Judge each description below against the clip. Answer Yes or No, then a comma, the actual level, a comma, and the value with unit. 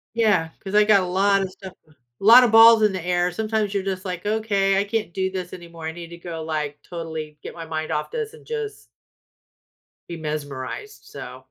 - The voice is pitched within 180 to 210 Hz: Yes, high, 190 Hz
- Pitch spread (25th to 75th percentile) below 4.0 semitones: No, average, 4.3 semitones